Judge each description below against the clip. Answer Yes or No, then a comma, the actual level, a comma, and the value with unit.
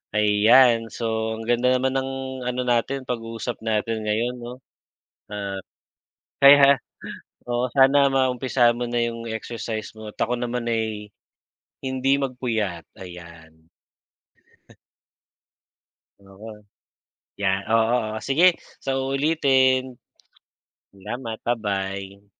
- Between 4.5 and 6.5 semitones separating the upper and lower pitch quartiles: No, average, 3.4 semitones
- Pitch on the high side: No, low, 115 Hz